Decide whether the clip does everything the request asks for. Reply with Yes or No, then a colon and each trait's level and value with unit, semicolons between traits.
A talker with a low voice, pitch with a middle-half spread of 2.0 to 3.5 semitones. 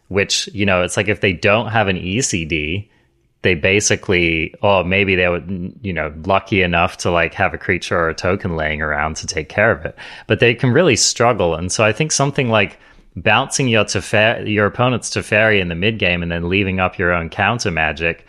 No: very low, 95 Hz; average, 3.9 semitones